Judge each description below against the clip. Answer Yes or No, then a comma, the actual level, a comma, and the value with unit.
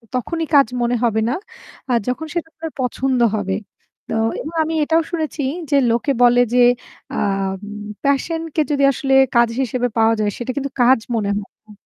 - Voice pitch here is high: Yes, very high, 250 Hz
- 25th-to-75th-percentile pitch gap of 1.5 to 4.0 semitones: No, average, 4.5 semitones